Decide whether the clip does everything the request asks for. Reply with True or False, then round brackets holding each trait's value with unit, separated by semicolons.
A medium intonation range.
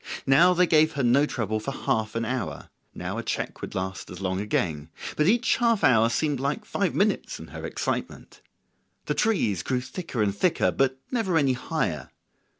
False (7.6 semitones)